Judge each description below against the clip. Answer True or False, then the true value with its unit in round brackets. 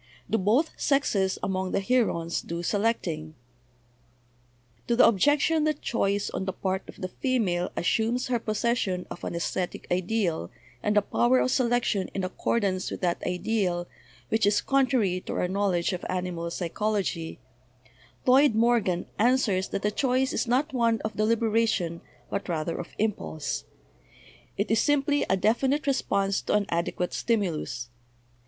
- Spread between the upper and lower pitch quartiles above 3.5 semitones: True (4.7 semitones)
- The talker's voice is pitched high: True (205 Hz)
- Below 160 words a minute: True (150 wpm)